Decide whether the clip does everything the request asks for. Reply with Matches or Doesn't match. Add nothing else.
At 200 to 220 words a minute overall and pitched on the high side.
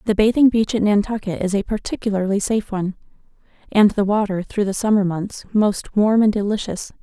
Doesn't match